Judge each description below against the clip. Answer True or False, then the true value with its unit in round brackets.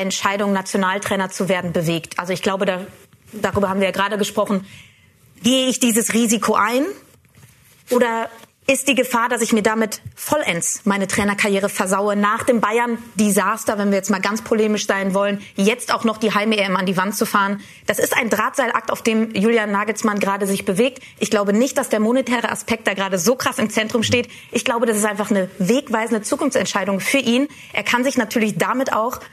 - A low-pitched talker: False (215 Hz)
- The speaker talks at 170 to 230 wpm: True (190 wpm)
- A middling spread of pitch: True (3.1 semitones)